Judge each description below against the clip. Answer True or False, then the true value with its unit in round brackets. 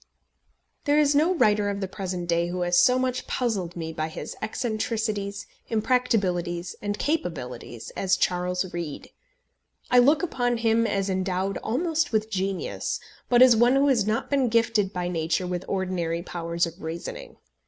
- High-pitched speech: True (200 Hz)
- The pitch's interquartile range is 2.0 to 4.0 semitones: False (5.3 semitones)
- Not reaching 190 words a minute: True (160 wpm)